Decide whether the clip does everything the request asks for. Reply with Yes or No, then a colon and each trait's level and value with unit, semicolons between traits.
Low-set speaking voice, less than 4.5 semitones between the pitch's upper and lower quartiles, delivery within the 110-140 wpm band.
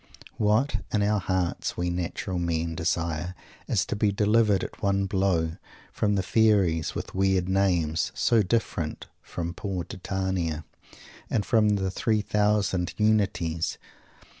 Yes: very low, 95 Hz; average, 3.3 semitones; slow, 135 wpm